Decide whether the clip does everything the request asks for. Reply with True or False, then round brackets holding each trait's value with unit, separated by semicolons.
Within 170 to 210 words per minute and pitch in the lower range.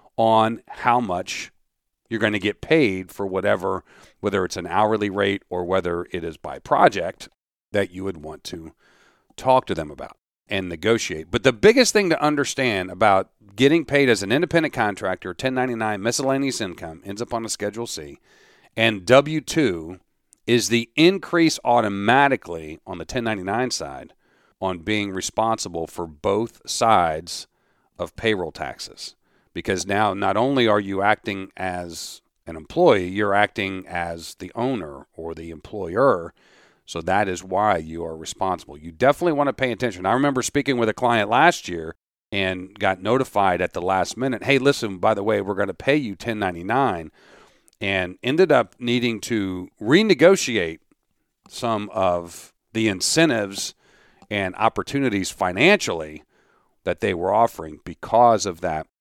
False (155 wpm; 105 Hz)